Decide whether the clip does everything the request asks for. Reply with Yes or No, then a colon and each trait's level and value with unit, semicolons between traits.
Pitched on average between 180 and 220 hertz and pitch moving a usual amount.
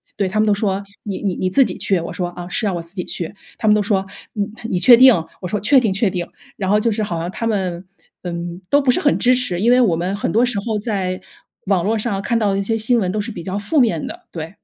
Yes: high, 200 Hz; average, 3.6 semitones